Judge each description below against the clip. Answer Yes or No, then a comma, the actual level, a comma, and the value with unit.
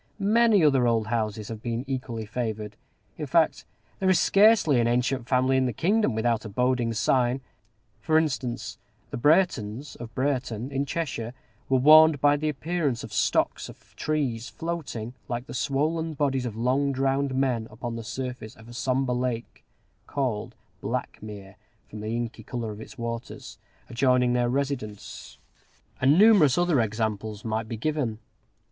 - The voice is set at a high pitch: No, low, 125 Hz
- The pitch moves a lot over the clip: No, average, 3.8 semitones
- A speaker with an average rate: Yes, average, 155 wpm